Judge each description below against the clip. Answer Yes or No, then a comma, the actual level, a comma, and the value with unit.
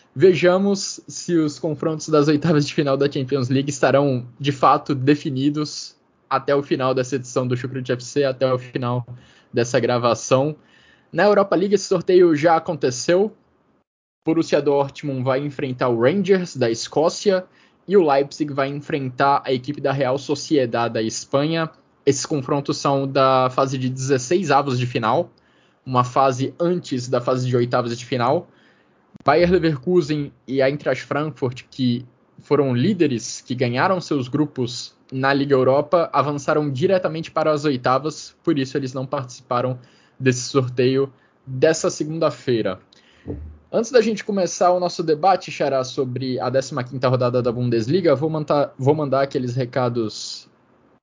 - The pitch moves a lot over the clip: No, average, 3.4 semitones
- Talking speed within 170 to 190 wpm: No, average, 145 wpm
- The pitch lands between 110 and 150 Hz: Yes, medium, 140 Hz